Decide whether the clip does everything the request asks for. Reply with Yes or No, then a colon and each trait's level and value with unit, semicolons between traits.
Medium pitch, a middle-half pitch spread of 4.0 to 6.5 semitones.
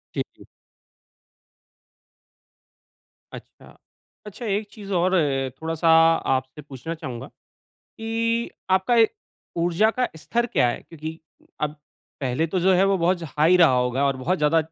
Yes: medium, 165 Hz; average, 4.9 semitones